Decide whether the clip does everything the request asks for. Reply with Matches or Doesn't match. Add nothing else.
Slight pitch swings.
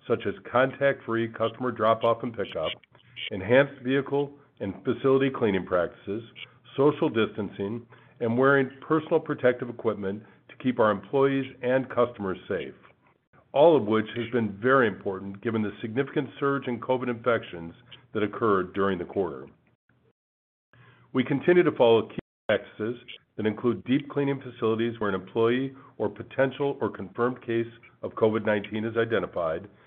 Doesn't match